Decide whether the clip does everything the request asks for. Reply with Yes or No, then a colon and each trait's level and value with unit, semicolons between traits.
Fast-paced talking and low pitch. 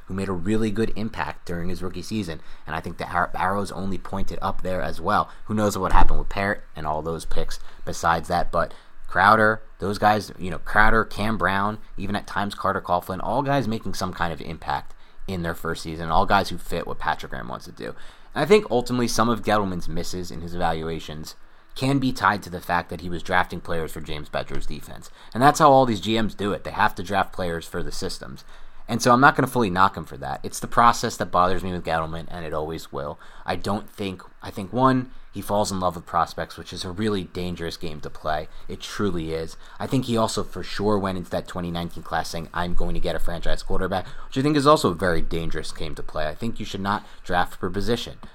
Yes: fast, 240 wpm; very low, 90 Hz